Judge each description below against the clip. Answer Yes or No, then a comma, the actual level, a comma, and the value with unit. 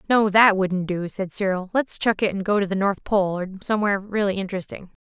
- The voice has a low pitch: No, high, 195 Hz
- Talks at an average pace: No, fast, 225 wpm